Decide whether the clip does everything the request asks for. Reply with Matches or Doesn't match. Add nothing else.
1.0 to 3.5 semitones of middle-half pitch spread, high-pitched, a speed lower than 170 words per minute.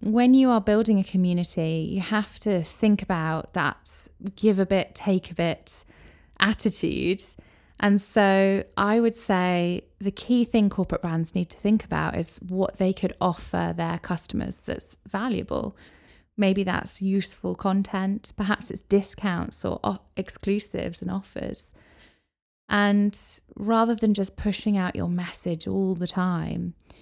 Matches